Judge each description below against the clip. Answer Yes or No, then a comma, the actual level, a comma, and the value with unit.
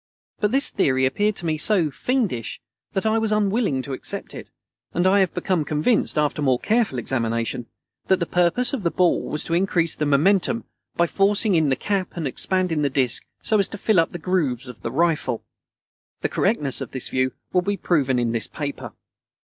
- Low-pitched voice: No, medium, 170 Hz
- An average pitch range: No, wide, 6.7 semitones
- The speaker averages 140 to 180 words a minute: No, average, 200 wpm